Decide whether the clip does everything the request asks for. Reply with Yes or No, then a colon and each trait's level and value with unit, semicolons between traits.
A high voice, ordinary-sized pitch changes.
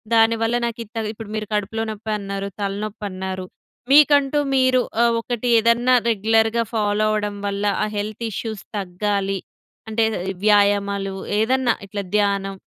No: high, 215 Hz; narrow, 2.2 semitones